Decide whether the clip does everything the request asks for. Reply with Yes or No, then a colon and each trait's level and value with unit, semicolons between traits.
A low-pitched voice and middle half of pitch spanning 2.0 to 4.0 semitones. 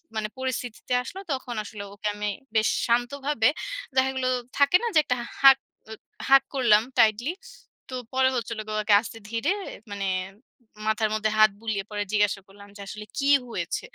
No: high, 225 Hz; average, 3.5 semitones